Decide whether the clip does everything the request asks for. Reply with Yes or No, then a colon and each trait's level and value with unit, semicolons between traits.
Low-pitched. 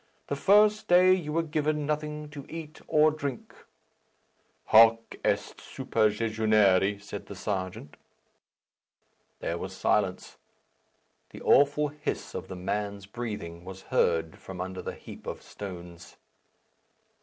Yes: low, 110 Hz